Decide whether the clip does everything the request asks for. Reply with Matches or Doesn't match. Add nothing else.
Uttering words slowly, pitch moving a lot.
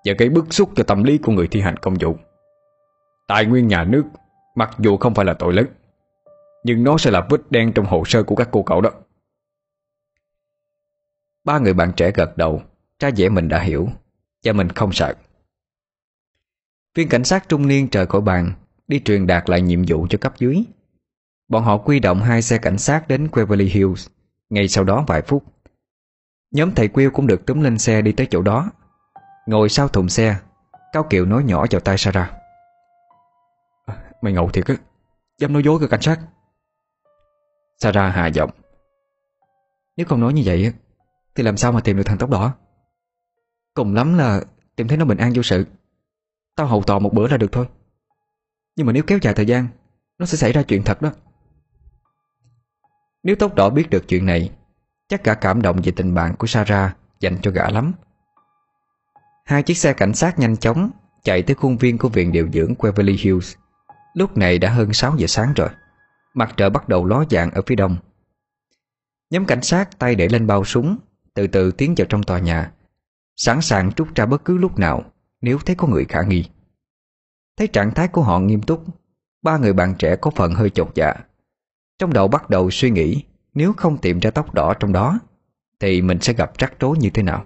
Doesn't match